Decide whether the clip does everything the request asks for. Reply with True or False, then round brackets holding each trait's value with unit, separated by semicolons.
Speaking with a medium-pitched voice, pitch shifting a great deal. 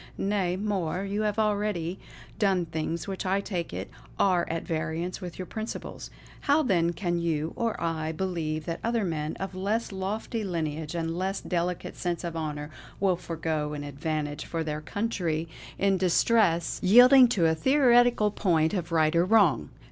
False (175 Hz; 3.9 semitones)